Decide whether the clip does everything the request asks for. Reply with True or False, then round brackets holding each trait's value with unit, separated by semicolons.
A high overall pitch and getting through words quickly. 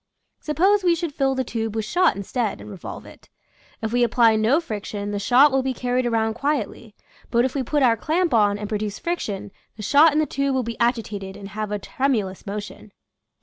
True (235 Hz; 220 wpm)